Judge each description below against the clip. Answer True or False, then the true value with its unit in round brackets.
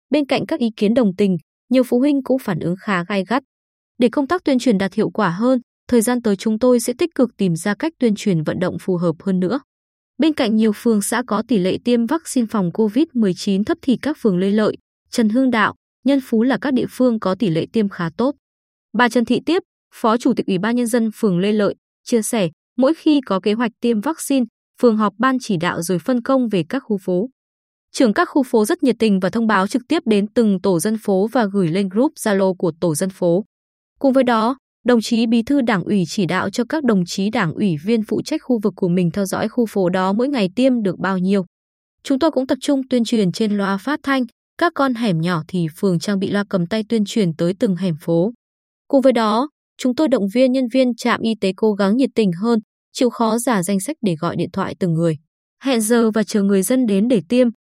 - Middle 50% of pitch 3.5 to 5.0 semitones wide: True (4.5 semitones)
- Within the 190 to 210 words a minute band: False (245 wpm)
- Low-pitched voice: False (225 Hz)